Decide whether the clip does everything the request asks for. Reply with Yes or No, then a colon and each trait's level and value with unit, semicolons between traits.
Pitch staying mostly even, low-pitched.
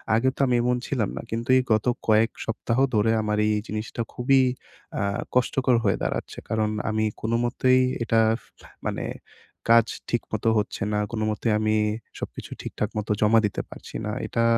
Yes: narrow, 2.0 semitones; low, 115 Hz